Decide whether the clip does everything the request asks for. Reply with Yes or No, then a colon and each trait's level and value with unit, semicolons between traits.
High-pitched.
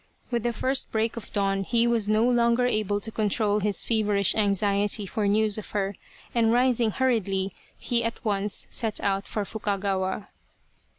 Yes: high, 215 Hz